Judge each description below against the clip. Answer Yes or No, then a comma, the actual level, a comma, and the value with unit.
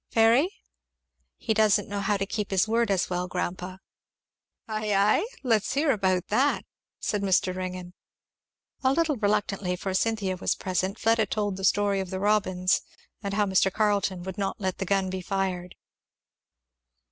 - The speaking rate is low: No, average, 160 wpm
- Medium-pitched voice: No, high, 200 Hz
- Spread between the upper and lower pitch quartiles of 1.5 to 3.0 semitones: Yes, narrow, 2.4 semitones